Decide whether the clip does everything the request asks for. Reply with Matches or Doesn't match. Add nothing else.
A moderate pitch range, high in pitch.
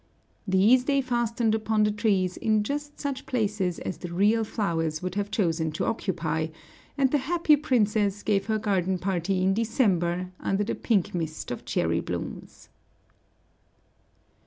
Matches